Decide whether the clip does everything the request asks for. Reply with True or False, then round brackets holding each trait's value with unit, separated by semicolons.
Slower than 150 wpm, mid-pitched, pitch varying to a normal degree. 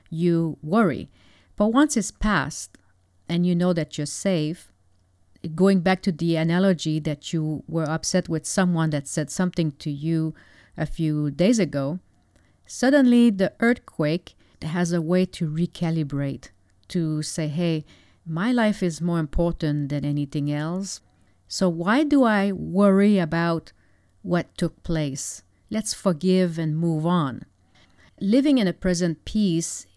True (140 wpm; 165 Hz; 4.1 semitones)